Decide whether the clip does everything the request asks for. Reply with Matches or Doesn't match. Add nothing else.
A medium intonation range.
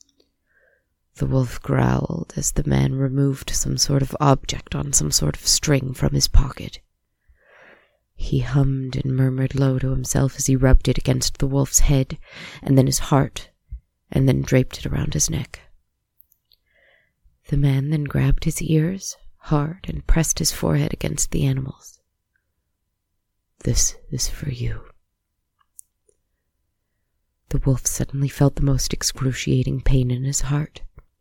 Matches